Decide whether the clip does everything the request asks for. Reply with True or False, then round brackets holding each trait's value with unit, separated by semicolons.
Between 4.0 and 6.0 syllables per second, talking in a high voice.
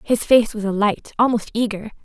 True (5.2 syllables/s; 220 Hz)